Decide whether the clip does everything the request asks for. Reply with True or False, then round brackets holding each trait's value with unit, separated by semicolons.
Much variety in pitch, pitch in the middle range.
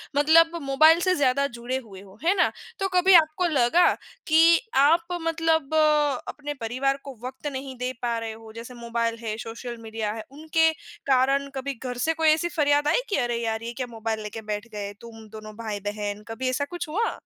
False (5.8 semitones; 260 Hz)